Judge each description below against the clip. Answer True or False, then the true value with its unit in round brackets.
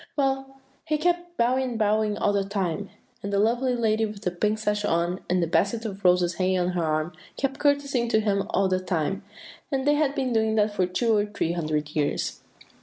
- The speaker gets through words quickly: True (215 wpm)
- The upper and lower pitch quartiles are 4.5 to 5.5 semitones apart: True (5.2 semitones)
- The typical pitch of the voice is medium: False (210 Hz)